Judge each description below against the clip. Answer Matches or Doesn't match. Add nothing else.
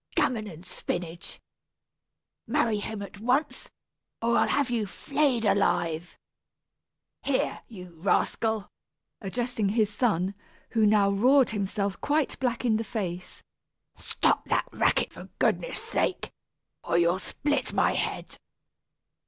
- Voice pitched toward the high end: Matches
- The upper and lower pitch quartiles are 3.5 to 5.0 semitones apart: Matches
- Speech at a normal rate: Doesn't match